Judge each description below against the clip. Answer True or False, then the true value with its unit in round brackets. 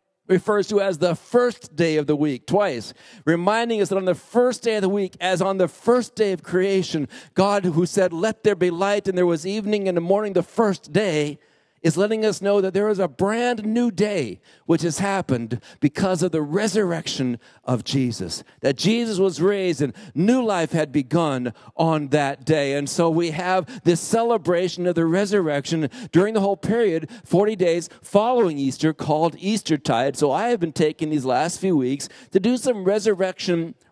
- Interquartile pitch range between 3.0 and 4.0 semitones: False (4.4 semitones)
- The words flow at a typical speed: True (190 wpm)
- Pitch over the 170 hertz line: True (185 Hz)